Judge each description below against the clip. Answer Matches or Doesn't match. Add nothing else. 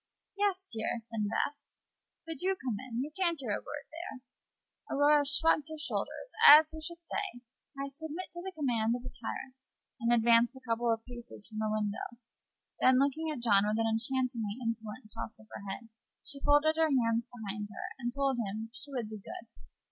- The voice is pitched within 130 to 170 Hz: Doesn't match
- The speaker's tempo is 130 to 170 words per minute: Doesn't match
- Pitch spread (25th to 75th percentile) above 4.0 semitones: Matches